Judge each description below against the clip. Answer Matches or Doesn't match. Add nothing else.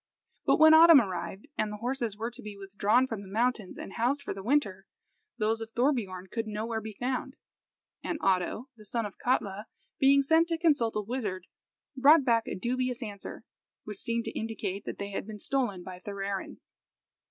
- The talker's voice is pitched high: Matches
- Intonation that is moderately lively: Matches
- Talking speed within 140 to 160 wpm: Doesn't match